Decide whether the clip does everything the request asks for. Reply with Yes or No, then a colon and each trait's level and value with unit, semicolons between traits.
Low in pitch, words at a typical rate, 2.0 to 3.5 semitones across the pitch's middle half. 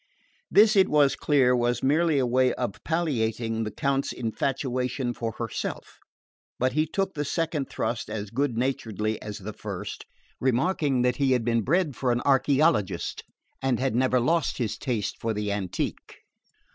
No: low, 125 Hz; average, 160 wpm; average, 3.9 semitones